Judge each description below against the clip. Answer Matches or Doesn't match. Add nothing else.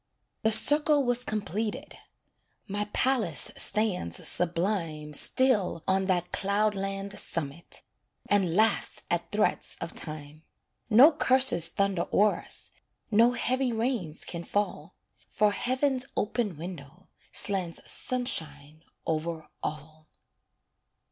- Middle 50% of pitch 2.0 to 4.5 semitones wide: Doesn't match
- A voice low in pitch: Doesn't match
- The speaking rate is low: Matches